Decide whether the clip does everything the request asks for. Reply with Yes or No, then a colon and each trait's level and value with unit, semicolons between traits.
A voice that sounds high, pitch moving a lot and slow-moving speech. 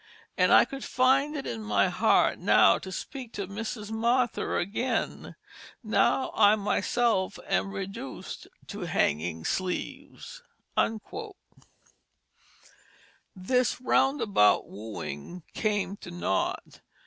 Yes: high, 205 Hz; wide, 5.8 semitones; slow, 100 wpm